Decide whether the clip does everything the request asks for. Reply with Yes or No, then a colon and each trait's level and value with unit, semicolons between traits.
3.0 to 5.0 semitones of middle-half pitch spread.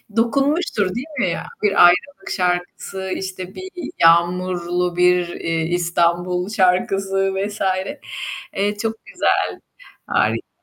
No: narrow, 2.5 semitones